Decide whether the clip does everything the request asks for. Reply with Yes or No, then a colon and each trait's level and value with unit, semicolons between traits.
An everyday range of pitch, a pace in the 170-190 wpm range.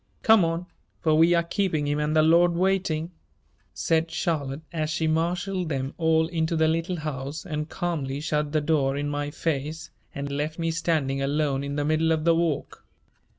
No: narrow, 2.3 semitones; average, 185 wpm